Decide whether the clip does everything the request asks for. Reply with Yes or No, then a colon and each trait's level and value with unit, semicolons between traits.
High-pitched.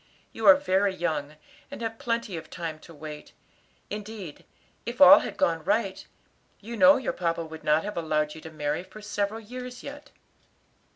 Yes: high, 195 Hz